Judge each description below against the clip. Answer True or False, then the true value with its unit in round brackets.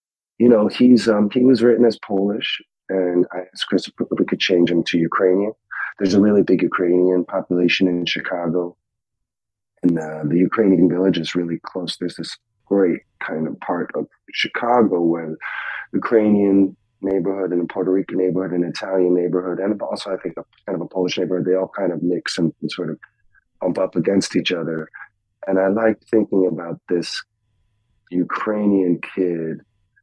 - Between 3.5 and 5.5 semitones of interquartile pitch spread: False (2.7 semitones)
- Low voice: True (95 Hz)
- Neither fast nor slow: True (175 wpm)